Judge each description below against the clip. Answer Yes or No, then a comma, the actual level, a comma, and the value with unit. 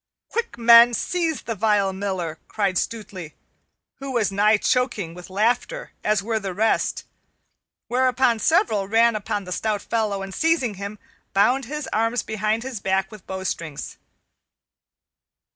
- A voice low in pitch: No, high, 215 Hz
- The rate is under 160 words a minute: Yes, average, 140 wpm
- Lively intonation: No, average, 3.5 semitones